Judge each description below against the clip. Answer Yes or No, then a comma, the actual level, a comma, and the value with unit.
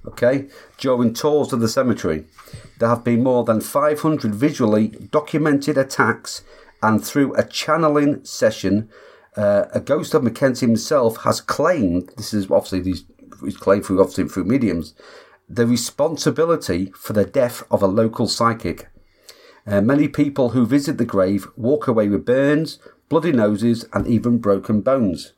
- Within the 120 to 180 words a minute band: Yes, average, 150 wpm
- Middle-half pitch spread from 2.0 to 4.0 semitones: No, wide, 5.4 semitones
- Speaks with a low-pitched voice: Yes, low, 120 Hz